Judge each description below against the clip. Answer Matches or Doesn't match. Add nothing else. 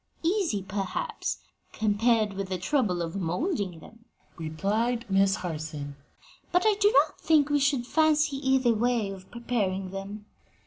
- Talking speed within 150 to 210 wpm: Doesn't match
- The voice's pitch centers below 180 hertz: Doesn't match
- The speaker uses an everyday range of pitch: Doesn't match